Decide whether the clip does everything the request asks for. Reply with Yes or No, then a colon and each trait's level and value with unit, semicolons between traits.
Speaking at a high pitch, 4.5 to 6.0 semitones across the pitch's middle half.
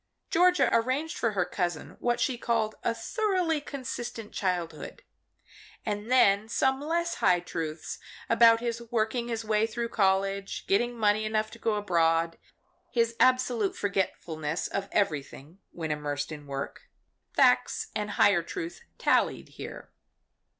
Yes: high, 215 Hz; average, 5.0 semitones